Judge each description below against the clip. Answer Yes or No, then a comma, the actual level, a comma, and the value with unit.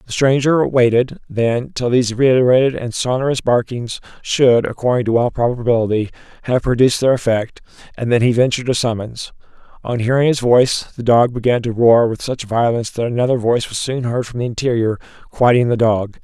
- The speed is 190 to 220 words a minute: No, average, 180 wpm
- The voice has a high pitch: No, low, 120 Hz